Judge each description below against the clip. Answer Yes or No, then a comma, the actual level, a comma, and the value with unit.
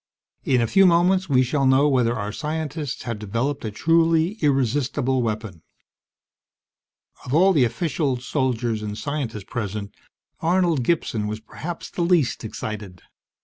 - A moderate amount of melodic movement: No, wide, 6.1 semitones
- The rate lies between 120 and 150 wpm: Yes, average, 140 wpm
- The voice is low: Yes, low, 130 Hz